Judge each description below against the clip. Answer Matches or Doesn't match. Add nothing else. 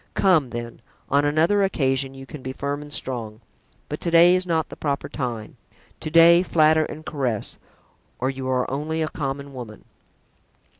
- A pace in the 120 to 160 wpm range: Doesn't match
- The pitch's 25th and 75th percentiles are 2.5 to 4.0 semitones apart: Matches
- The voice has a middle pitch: Matches